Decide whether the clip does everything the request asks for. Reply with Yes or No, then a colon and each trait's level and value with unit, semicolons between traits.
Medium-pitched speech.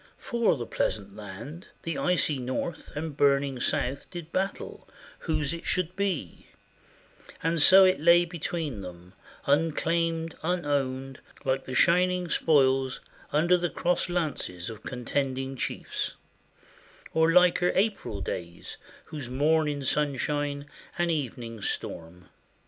Yes: medium, 150 Hz